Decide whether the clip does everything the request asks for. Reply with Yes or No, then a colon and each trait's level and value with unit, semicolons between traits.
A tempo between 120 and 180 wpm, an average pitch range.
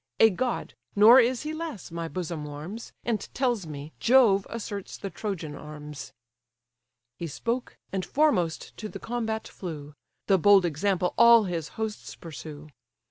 No: average, 145 wpm; wide, 6.2 semitones